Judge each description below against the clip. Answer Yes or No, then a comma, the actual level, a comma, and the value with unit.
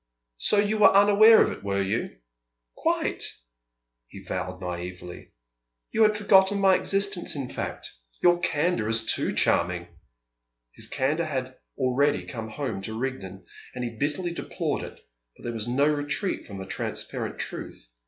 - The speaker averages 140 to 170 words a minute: Yes, average, 155 wpm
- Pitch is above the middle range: No, low, 135 Hz